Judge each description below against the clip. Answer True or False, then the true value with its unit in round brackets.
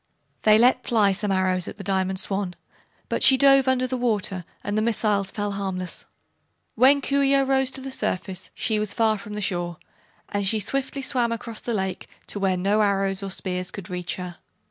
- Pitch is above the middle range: True (205 Hz)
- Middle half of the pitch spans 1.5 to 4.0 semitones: False (4.4 semitones)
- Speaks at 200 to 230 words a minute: True (205 wpm)